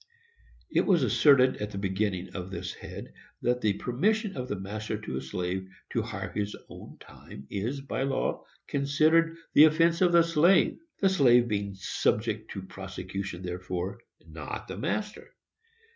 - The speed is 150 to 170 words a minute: Yes, average, 160 wpm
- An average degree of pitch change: No, wide, 8.0 semitones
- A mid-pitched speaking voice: No, low, 110 Hz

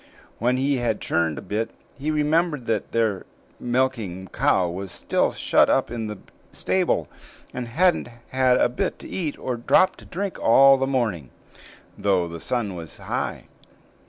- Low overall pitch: Yes, low, 120 Hz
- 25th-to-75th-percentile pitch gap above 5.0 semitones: Yes, wide, 5.6 semitones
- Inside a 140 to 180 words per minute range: Yes, average, 165 wpm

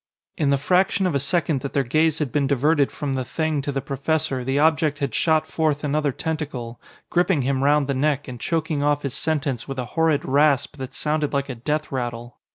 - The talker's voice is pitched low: No, medium, 145 Hz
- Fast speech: Yes, fast, 215 wpm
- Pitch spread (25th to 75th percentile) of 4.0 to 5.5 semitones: No, narrow, 2.5 semitones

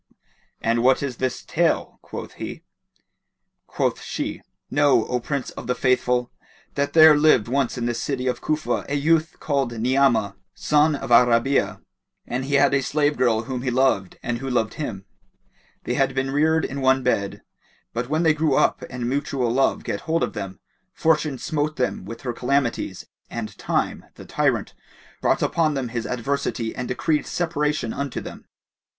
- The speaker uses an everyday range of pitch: Yes, average, 3.3 semitones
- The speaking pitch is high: No, low, 130 Hz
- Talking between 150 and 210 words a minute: Yes, average, 175 wpm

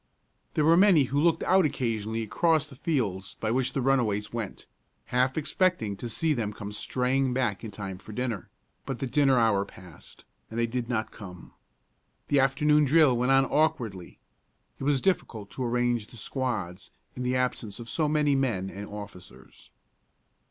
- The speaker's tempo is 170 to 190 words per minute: Yes, average, 175 wpm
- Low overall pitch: Yes, low, 125 Hz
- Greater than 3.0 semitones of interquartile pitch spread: Yes, average, 4.7 semitones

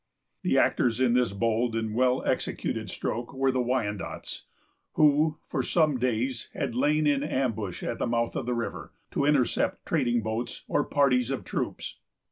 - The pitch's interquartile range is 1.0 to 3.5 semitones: Yes, average, 2.7 semitones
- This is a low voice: Yes, low, 125 Hz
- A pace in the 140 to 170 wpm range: Yes, average, 165 wpm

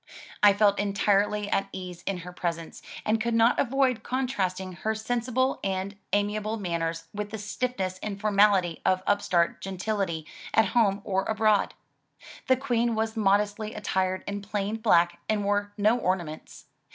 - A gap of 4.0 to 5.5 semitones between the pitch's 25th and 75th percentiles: No, average, 2.7 semitones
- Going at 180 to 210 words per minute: No, average, 150 wpm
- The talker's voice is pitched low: No, high, 205 Hz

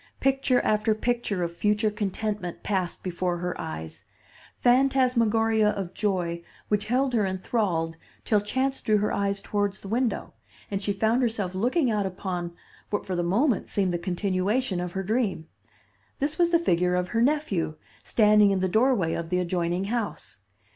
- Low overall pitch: No, high, 205 Hz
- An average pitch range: Yes, average, 4.2 semitones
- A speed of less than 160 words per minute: No, average, 165 wpm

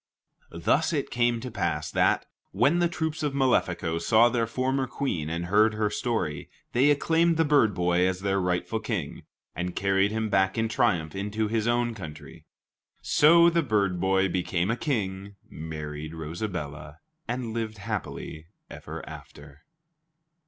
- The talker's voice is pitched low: Yes, low, 105 Hz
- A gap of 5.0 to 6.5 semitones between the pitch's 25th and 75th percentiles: Yes, wide, 5.5 semitones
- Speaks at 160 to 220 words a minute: No, average, 150 wpm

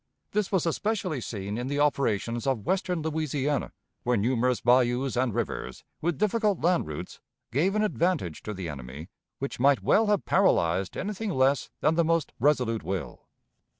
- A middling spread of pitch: No, wide, 7.1 semitones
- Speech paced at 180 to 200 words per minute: No, average, 160 wpm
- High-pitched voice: No, low, 135 Hz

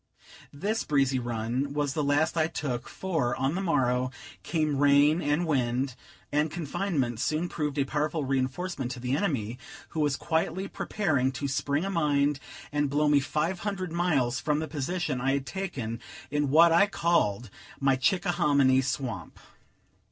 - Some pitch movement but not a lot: Yes, average, 3.7 semitones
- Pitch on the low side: No, medium, 145 Hz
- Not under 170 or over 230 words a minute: No, average, 160 wpm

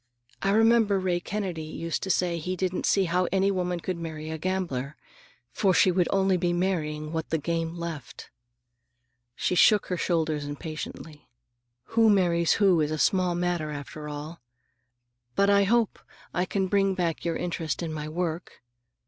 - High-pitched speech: No, medium, 175 Hz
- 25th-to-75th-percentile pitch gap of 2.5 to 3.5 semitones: Yes, average, 3.0 semitones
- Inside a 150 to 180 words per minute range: Yes, average, 165 wpm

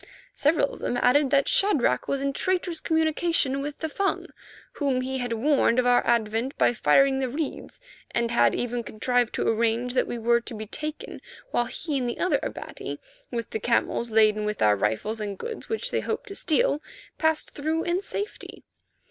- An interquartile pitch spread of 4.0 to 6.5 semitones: Yes, average, 4.9 semitones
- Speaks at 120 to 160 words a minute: No, average, 190 wpm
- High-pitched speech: Yes, very high, 260 Hz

